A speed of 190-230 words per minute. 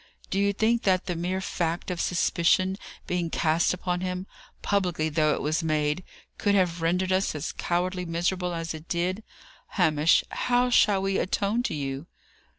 No: average, 165 wpm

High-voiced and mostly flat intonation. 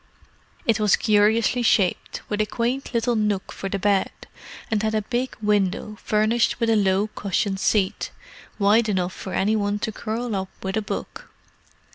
Yes: high, 210 Hz; narrow, 2.1 semitones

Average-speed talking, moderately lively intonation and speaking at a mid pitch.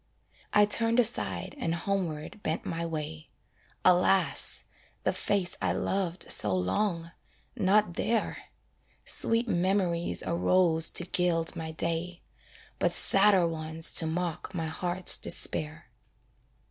No: slow, 115 wpm; average, 3.0 semitones; medium, 175 Hz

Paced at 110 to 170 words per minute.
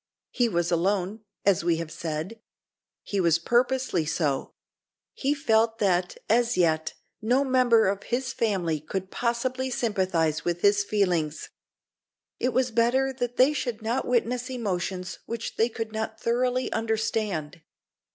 Yes: average, 140 wpm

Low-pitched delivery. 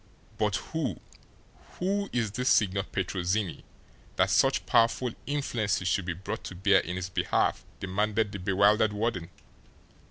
Yes: low, 100 Hz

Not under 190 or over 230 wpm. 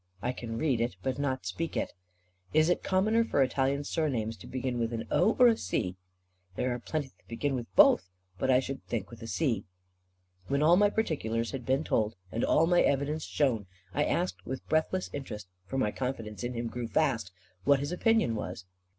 Yes: fast, 205 wpm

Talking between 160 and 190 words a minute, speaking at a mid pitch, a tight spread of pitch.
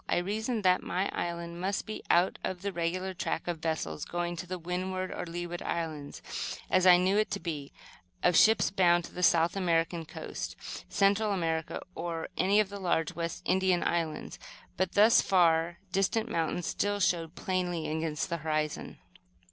Yes: average, 170 wpm; medium, 175 Hz; narrow, 2.2 semitones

